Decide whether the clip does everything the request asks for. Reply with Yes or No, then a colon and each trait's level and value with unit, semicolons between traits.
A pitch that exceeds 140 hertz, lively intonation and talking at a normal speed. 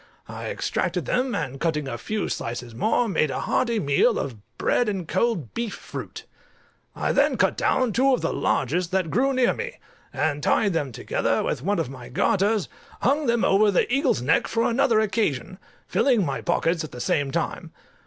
Yes: high, 190 Hz; wide, 8.6 semitones; average, 185 wpm